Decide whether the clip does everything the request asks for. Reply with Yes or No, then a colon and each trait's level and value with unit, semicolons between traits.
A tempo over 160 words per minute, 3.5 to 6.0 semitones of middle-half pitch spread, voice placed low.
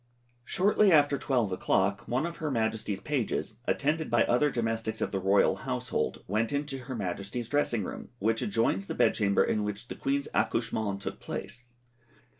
Yes: average, 170 wpm; average, 5.1 semitones; low, 115 Hz